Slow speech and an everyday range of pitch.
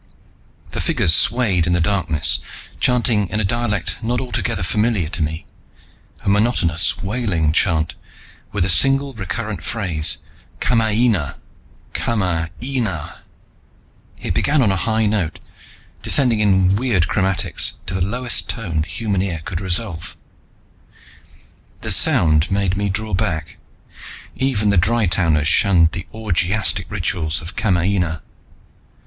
Yes: slow, 130 wpm; average, 4.7 semitones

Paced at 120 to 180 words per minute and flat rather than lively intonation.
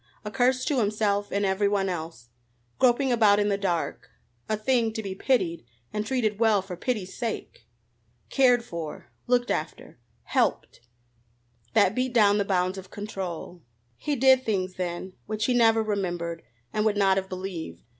No: average, 160 wpm; average, 3.9 semitones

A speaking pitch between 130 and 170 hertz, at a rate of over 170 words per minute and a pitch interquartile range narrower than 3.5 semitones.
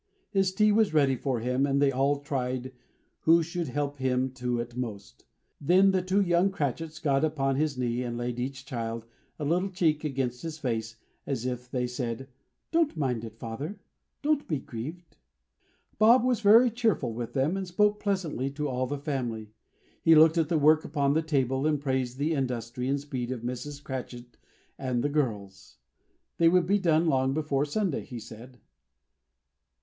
No: medium, 140 Hz; average, 180 wpm; average, 4.7 semitones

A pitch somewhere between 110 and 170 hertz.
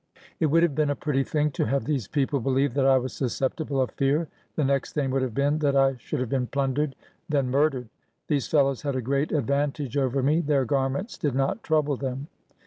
Yes: medium, 140 Hz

